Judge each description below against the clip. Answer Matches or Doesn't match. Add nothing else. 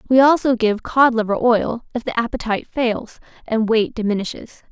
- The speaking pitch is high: Matches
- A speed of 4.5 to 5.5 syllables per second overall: Matches